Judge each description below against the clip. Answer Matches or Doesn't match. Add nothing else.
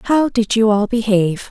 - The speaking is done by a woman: Matches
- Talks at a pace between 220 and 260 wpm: Doesn't match